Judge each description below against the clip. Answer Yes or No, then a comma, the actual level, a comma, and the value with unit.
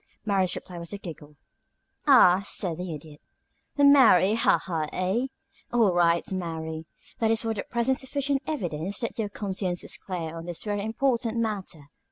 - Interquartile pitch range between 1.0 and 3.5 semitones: No, average, 5.2 semitones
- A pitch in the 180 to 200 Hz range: Yes, high, 190 Hz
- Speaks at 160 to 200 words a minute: Yes, average, 170 wpm